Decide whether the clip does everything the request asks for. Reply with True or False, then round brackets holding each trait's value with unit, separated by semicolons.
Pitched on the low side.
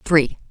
False (150 Hz)